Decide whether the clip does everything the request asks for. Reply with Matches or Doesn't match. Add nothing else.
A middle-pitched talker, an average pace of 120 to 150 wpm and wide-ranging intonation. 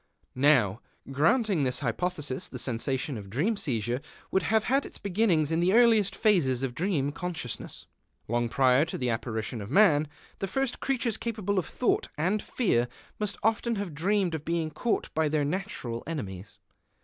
Doesn't match